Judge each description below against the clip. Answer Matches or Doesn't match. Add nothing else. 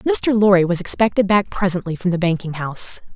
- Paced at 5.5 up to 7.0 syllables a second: Matches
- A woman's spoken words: Matches